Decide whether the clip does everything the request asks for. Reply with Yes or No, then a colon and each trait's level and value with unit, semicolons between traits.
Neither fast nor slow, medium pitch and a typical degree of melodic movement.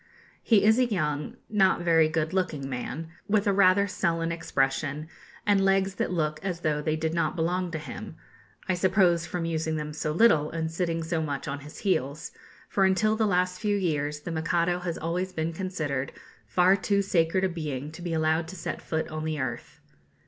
Yes: average, 195 wpm; medium, 165 Hz; average, 3.2 semitones